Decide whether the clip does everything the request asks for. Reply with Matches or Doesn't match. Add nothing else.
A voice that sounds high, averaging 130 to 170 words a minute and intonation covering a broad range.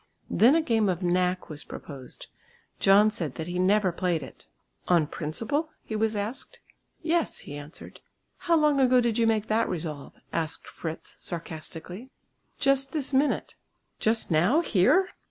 Matches